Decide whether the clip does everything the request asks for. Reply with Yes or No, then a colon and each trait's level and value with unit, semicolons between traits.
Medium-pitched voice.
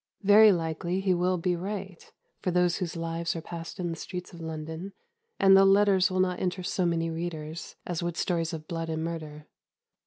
Yes: medium, 175 Hz